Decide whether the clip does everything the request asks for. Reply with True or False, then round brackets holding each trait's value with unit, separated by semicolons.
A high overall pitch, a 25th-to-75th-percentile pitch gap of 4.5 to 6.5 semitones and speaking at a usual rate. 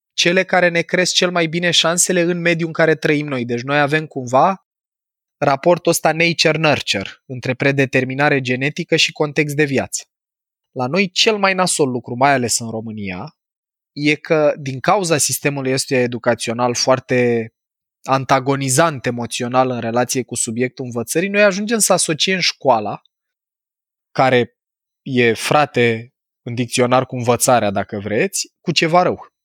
False (140 Hz; 5.2 semitones; 145 wpm)